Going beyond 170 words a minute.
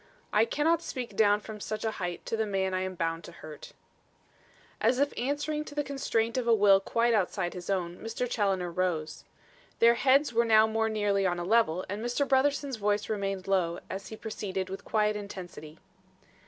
Yes: average, 195 wpm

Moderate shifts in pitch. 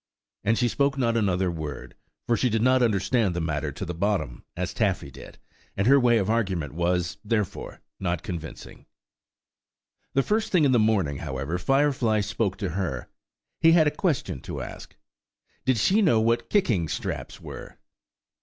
No: wide, 6.4 semitones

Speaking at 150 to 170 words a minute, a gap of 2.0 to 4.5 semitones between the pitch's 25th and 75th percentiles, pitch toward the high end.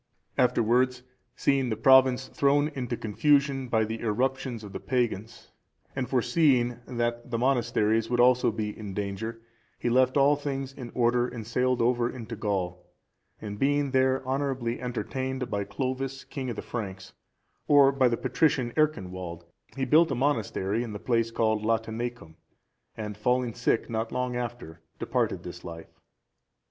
No: average, 155 wpm; average, 2.9 semitones; low, 120 Hz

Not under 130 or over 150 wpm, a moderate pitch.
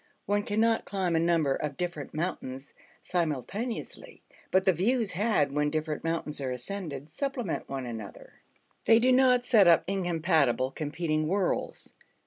Yes: average, 140 wpm; medium, 170 Hz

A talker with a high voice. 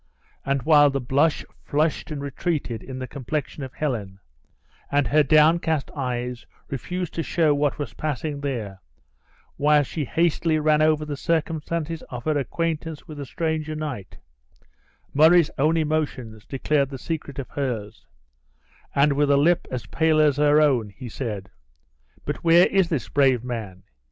No: medium, 145 Hz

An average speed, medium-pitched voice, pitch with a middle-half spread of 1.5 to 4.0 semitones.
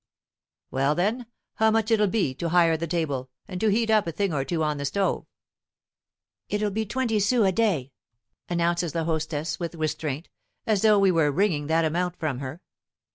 No: average, 185 wpm; medium, 170 Hz; average, 5.0 semitones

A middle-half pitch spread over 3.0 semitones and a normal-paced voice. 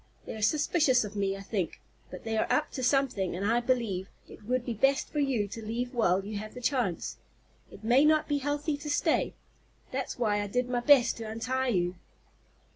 No: average, 4.7 semitones; fast, 210 wpm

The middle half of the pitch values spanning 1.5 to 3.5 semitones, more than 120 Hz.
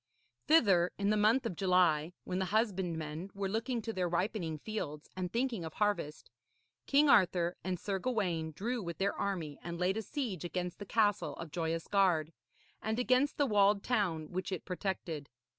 No: average, 4.0 semitones; high, 190 Hz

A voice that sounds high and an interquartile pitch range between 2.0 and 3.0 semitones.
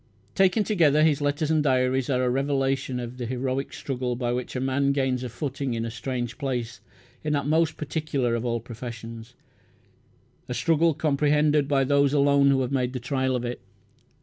No: low, 135 Hz; narrow, 2.6 semitones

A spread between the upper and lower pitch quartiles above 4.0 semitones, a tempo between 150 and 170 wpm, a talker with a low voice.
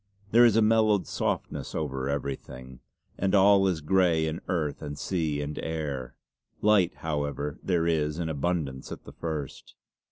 Yes: average, 4.5 semitones; average, 155 wpm; very low, 80 Hz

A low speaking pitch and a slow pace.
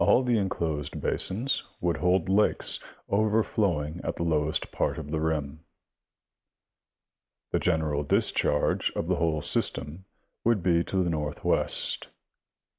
Yes: very low, 85 Hz; slow, 125 wpm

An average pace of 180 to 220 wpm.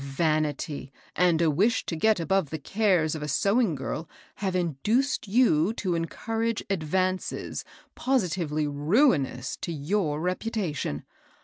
No: slow, 135 wpm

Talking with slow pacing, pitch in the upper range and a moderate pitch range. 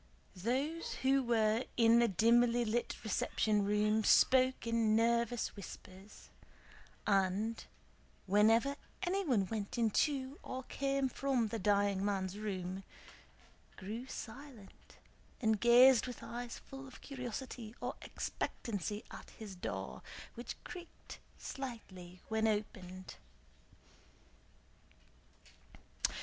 Yes: slow, 100 wpm; high, 225 Hz; average, 3.7 semitones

